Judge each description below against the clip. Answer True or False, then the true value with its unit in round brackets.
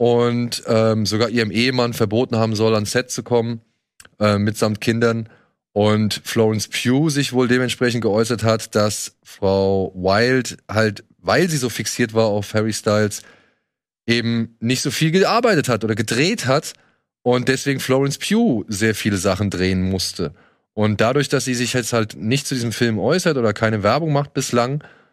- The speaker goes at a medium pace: True (165 wpm)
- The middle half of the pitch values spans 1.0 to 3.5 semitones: True (2.7 semitones)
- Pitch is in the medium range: False (115 Hz)